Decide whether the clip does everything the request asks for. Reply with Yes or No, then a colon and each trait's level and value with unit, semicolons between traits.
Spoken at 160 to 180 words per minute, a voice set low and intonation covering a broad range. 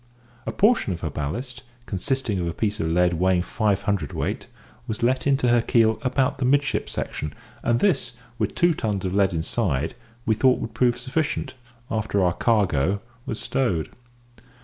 Yes: average, 170 wpm; low, 110 Hz; wide, 5.8 semitones